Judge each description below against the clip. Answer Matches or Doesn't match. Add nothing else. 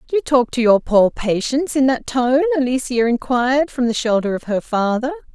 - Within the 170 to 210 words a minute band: Matches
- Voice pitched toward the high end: Matches